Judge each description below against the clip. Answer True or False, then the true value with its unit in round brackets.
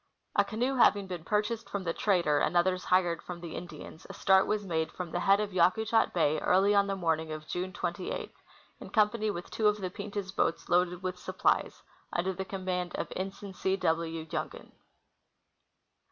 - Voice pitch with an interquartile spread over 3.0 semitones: False (2.7 semitones)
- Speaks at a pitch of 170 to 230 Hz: True (185 Hz)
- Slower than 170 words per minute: False (190 wpm)